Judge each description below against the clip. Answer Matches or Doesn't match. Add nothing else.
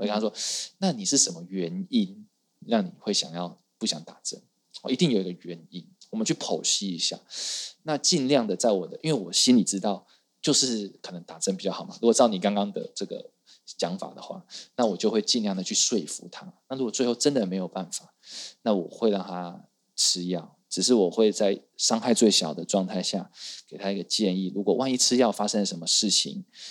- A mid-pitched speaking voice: Doesn't match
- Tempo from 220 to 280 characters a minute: Doesn't match